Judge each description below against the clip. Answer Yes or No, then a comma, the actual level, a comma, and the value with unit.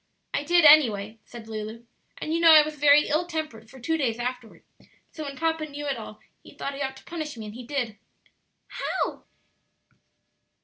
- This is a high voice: Yes, very high, 280 Hz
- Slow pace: No, average, 190 wpm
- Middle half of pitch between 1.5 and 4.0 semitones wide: No, average, 5.1 semitones